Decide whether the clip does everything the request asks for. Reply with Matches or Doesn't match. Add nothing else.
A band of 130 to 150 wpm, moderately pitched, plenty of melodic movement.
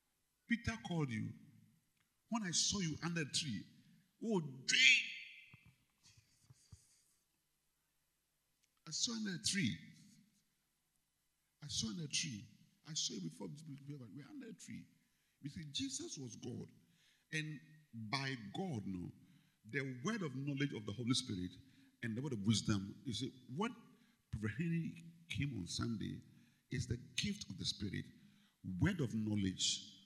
Matches